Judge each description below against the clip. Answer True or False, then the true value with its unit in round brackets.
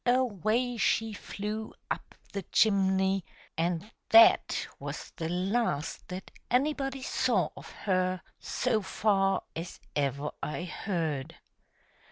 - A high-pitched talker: True (195 Hz)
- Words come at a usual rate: False (115 wpm)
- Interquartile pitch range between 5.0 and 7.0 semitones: False (4.1 semitones)